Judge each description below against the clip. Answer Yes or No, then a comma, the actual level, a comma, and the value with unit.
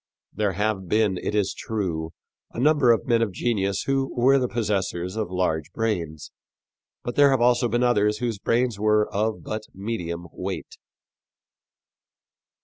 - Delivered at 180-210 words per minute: No, average, 150 wpm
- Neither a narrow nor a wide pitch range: Yes, average, 3.8 semitones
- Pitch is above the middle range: No, low, 105 Hz